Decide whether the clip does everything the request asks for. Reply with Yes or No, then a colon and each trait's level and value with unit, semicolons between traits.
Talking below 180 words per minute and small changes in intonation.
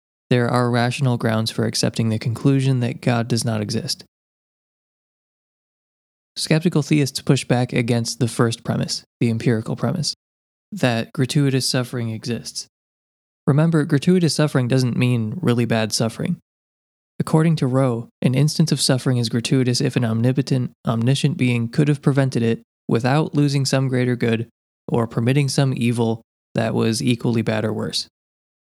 No: average, 145 wpm; average, 3.3 semitones